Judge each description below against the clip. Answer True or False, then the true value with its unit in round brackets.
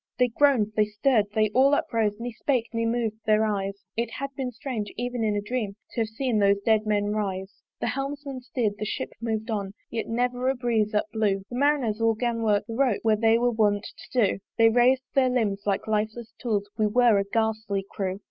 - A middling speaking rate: False (215 wpm)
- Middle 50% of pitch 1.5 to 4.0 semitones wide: True (2.7 semitones)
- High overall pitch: True (225 Hz)